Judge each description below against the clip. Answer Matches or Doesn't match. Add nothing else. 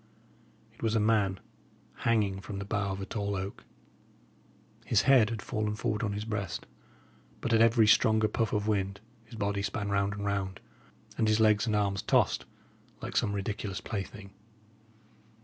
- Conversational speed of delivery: Matches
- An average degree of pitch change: Doesn't match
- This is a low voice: Matches